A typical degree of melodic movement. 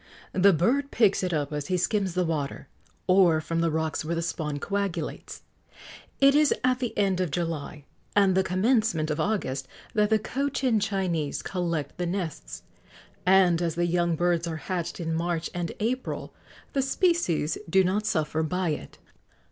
Yes: average, 4.0 semitones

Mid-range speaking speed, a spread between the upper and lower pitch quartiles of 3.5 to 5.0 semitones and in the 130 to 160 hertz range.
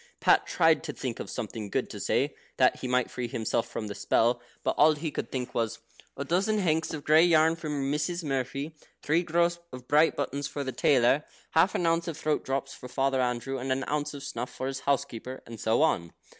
No: fast, 225 wpm; average, 4.0 semitones; medium, 140 Hz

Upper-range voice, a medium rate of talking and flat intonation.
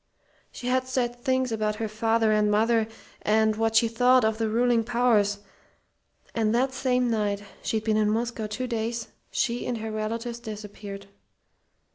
Yes: high, 225 Hz; average, 160 wpm; narrow, 2.0 semitones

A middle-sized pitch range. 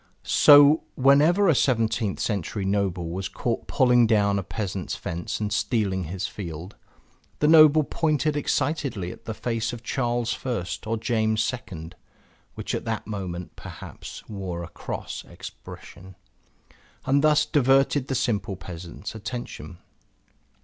No: wide, 5.8 semitones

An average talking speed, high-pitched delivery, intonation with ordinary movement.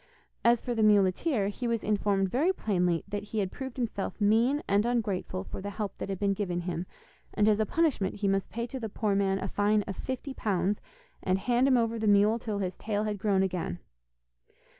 No: fast, 215 wpm; high, 205 Hz; average, 3.0 semitones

